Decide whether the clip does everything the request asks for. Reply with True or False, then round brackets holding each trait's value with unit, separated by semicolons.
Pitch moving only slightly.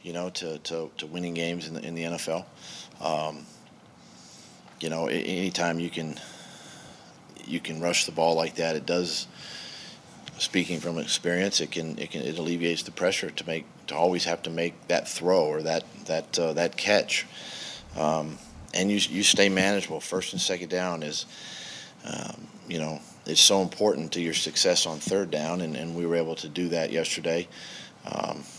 True (1.5 semitones)